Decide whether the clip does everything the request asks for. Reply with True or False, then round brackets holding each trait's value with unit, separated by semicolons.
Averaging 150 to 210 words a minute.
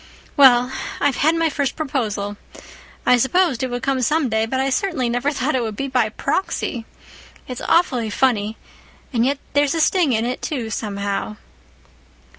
True (160 wpm)